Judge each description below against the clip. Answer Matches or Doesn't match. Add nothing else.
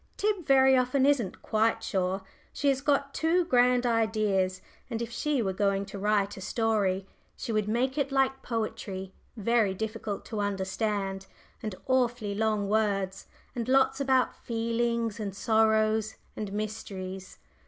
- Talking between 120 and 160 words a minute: Matches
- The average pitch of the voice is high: Matches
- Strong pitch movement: Doesn't match